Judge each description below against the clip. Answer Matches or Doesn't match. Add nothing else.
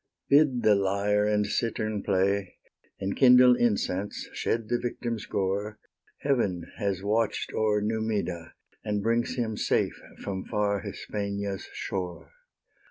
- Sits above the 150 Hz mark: Doesn't match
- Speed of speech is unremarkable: Doesn't match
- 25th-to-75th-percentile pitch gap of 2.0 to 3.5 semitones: Matches